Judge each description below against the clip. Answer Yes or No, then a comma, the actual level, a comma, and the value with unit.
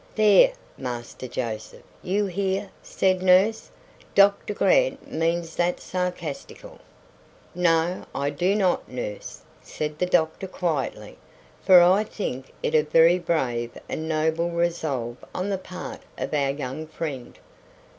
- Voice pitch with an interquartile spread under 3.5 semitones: No, average, 4.4 semitones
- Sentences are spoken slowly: Yes, slow, 125 wpm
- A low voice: No, medium, 170 Hz